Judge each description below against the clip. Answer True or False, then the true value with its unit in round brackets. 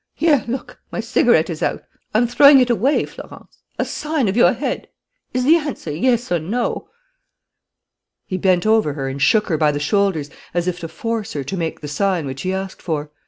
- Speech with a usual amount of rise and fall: False (7.4 semitones)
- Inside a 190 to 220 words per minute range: True (205 wpm)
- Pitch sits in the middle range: False (195 Hz)